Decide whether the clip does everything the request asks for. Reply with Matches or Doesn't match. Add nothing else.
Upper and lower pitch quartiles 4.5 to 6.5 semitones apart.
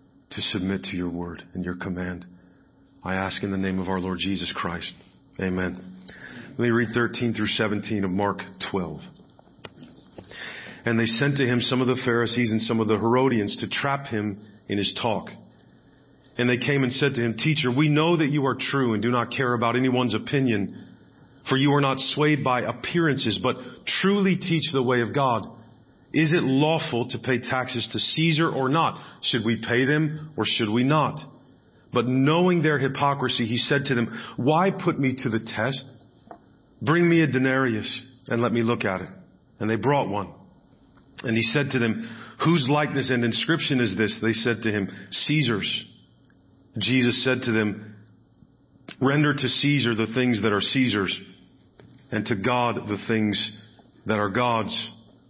Doesn't match